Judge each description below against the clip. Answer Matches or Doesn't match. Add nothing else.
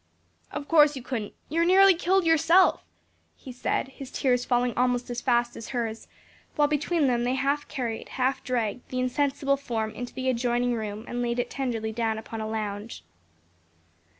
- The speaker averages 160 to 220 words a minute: Matches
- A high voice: Matches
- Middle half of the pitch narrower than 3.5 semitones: Matches